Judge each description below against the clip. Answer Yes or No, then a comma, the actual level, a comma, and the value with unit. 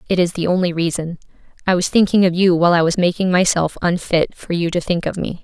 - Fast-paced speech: Yes, fast, 245 wpm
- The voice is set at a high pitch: No, medium, 175 Hz